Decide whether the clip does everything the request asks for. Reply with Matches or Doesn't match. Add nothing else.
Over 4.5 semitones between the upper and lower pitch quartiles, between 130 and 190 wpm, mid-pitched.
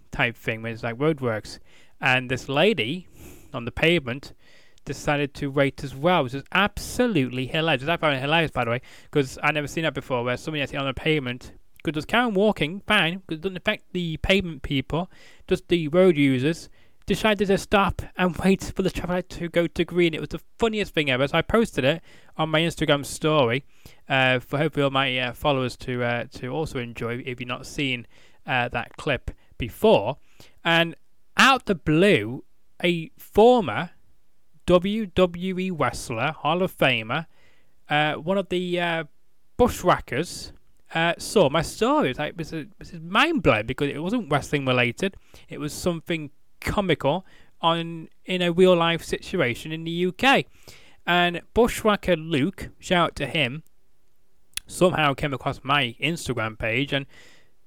Matches